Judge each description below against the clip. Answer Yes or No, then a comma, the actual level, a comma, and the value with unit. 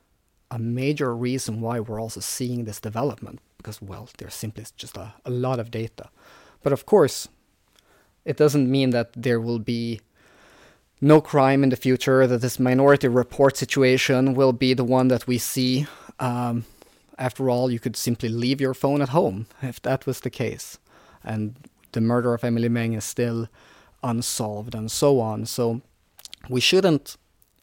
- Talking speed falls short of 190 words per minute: Yes, average, 165 wpm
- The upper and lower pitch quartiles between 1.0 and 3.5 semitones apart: Yes, narrow, 2.5 semitones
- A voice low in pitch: Yes, low, 125 Hz